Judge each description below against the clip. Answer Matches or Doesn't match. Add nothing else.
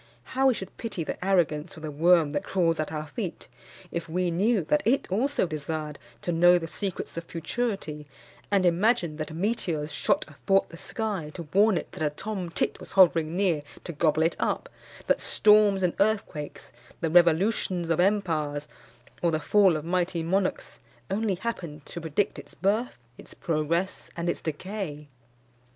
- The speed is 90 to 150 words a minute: Doesn't match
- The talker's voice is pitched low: Doesn't match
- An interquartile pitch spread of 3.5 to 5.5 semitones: Matches